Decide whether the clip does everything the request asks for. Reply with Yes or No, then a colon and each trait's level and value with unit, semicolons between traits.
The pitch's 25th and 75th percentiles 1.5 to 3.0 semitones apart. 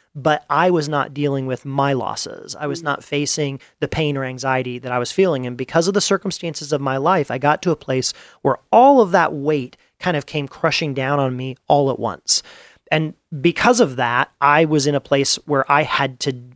No: average, 3.4 semitones